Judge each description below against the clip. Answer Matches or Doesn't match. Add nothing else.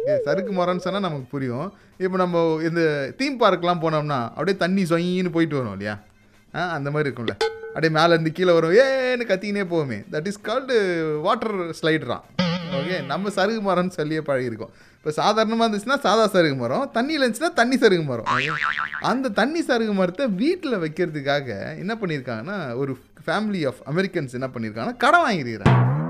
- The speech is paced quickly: Matches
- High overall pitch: Doesn't match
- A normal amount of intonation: Doesn't match